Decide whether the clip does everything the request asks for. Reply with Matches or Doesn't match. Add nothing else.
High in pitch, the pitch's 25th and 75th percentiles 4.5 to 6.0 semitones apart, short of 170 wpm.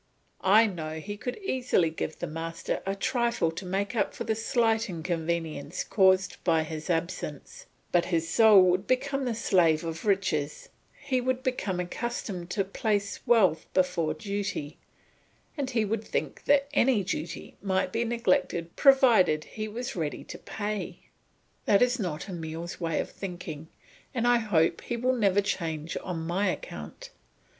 Matches